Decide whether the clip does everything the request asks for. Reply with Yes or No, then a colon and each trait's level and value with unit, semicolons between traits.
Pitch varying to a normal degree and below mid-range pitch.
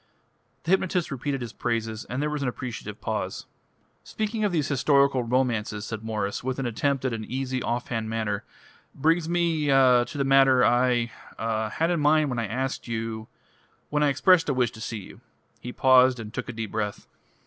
Yes: average, 3.9 semitones; low, 130 Hz